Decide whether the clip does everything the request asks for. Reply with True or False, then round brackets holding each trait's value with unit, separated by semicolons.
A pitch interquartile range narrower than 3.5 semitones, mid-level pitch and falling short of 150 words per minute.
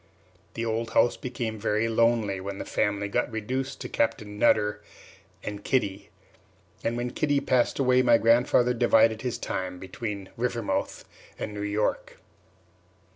False (2.9 semitones; 115 Hz; 140 wpm)